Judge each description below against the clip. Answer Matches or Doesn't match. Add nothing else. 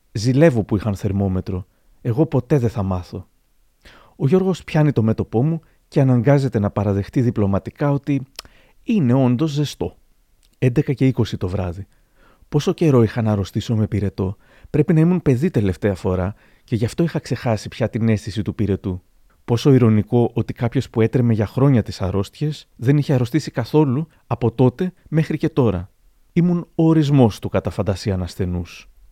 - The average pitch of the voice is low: Matches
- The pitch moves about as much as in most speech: Doesn't match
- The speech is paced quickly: Doesn't match